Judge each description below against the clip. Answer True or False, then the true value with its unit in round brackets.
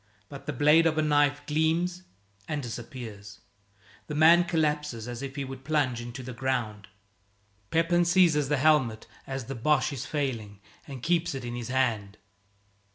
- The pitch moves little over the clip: False (4.3 semitones)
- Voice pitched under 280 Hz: True (140 Hz)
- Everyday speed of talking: True (160 wpm)